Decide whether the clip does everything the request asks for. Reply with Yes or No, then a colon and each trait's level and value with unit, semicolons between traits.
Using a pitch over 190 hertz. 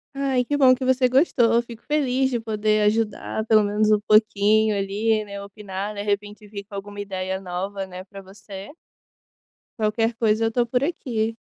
Yes: high, 215 Hz